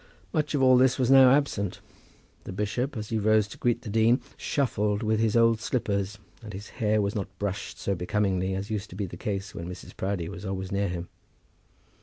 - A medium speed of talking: No, fast, 210 wpm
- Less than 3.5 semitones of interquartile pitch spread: Yes, average, 3.1 semitones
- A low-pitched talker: Yes, low, 105 Hz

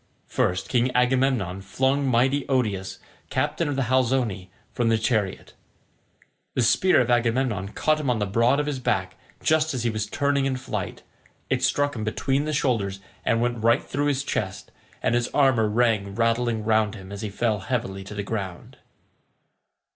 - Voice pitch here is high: No, low, 120 Hz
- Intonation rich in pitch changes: No, average, 4.0 semitones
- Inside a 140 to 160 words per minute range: No, average, 175 wpm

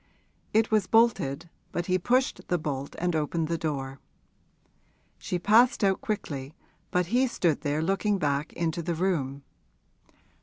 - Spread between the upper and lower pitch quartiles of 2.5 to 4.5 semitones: No, average, 5.1 semitones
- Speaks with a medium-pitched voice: Yes, medium, 170 Hz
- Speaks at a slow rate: No, average, 145 wpm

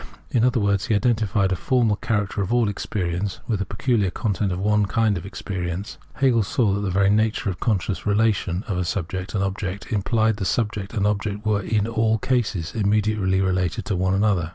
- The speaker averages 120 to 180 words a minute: No, average, 200 wpm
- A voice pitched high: No, low, 100 Hz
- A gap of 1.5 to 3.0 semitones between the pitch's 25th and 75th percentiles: Yes, narrow, 2.4 semitones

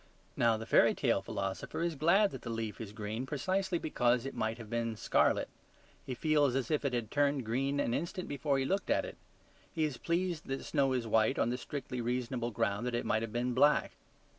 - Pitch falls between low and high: No, low, 125 Hz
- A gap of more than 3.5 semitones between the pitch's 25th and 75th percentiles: Yes, average, 4.2 semitones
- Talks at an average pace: No, fast, 215 wpm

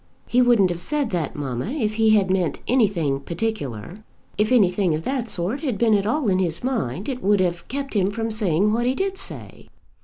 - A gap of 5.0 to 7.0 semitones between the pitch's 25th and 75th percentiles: Yes, wide, 5.4 semitones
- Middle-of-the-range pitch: No, high, 205 Hz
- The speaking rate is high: Yes, fast, 210 wpm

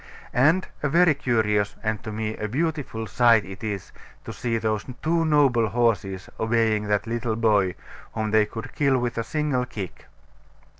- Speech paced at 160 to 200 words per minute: Yes, average, 165 wpm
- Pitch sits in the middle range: No, low, 115 Hz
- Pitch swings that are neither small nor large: Yes, average, 3.4 semitones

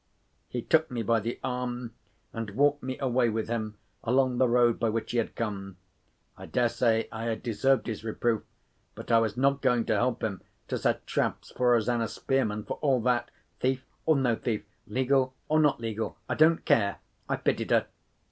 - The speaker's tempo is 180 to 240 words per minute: Yes, average, 185 wpm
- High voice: No, low, 120 Hz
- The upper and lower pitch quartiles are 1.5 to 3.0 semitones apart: Yes, narrow, 2.5 semitones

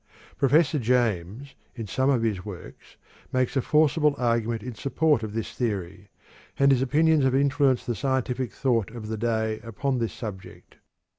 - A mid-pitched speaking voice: No, low, 125 Hz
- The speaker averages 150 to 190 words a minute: Yes, average, 160 wpm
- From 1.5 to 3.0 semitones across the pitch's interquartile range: No, average, 3.8 semitones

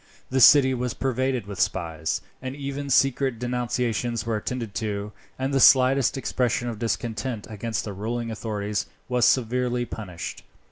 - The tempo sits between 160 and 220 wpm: No, average, 145 wpm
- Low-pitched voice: Yes, low, 120 Hz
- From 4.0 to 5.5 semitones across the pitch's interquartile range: No, average, 3.2 semitones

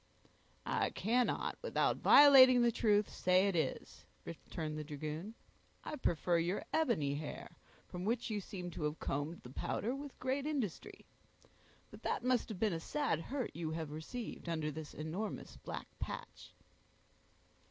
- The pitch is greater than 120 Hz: Yes, medium, 185 Hz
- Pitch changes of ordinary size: No, wide, 7.3 semitones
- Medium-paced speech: Yes, average, 155 wpm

